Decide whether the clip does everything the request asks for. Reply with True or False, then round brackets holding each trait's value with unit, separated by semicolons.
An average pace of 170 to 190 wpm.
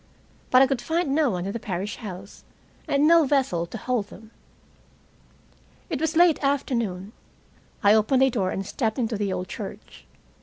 True (175 wpm)